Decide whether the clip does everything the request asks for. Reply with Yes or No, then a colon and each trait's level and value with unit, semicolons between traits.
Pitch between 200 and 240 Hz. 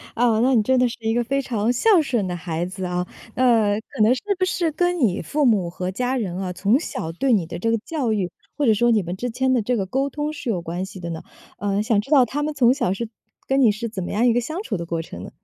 Yes: high, 225 Hz